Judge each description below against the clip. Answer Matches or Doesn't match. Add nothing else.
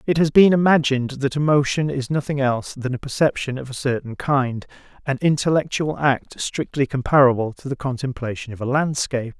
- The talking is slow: Doesn't match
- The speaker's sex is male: Matches